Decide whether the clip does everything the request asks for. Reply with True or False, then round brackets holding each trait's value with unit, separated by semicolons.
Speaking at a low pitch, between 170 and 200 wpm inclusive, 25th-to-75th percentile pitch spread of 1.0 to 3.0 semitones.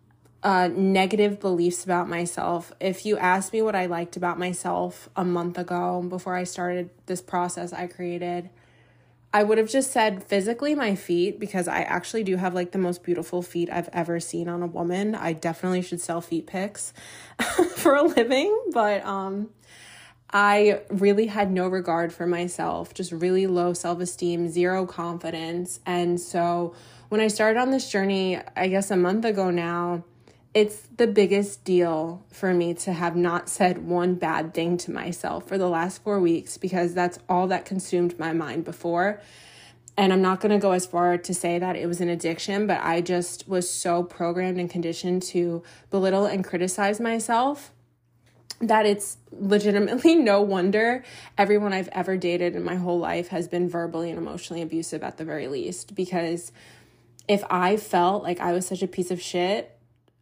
False (180 Hz; 175 wpm; 2.4 semitones)